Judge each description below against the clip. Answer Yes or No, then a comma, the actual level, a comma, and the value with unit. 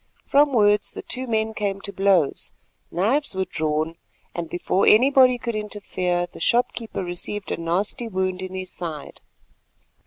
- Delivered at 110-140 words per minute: No, average, 150 wpm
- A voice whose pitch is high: Yes, high, 195 Hz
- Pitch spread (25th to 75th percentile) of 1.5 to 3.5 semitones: No, average, 4.0 semitones